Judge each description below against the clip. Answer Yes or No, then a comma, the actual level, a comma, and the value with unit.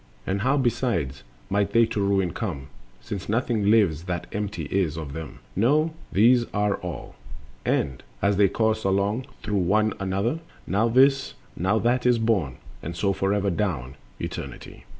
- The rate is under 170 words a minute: Yes, average, 155 wpm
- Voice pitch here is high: No, low, 100 Hz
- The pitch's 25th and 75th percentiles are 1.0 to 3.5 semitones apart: No, average, 4.2 semitones